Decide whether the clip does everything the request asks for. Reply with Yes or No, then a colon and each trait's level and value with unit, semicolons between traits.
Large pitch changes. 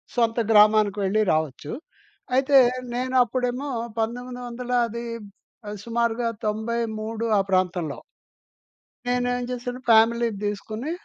No: narrow, 2.4 semitones